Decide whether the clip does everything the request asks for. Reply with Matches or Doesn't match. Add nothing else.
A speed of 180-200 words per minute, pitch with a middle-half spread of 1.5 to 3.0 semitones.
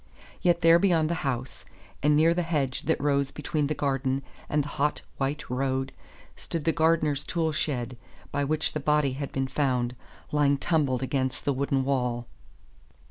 Doesn't match